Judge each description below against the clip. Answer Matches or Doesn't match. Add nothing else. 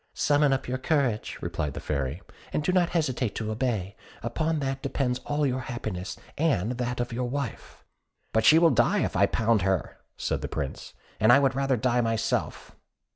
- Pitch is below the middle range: Matches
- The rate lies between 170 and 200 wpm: Matches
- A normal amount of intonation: Matches